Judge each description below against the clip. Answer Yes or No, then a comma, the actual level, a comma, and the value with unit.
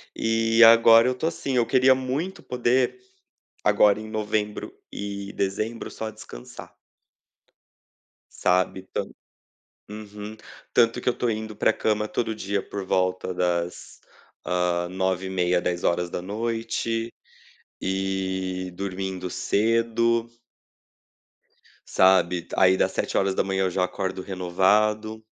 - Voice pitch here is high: No, low, 105 Hz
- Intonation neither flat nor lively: Yes, average, 3.5 semitones